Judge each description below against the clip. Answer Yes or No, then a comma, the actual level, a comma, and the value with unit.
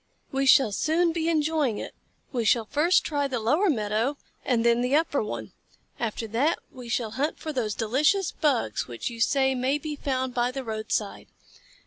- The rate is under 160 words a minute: No, average, 180 wpm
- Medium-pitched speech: No, very high, 260 Hz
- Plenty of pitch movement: No, average, 4.6 semitones